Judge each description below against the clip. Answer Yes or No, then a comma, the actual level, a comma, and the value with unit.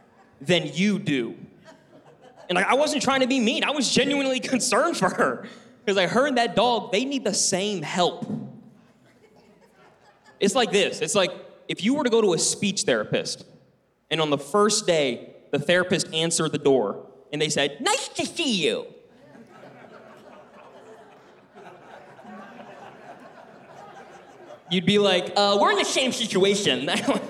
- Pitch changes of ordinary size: No, wide, 6.2 semitones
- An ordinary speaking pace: Yes, average, 150 wpm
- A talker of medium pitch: No, high, 205 Hz